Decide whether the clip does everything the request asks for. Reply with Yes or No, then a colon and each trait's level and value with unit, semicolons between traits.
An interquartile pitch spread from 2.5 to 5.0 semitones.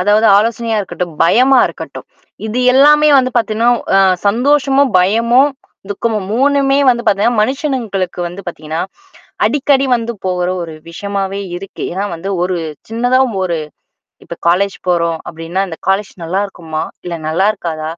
No: wide, 5.4 semitones